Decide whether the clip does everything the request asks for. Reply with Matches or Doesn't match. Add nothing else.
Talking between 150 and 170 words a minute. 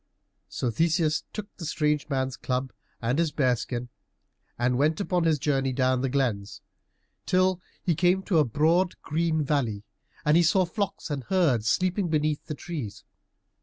Matches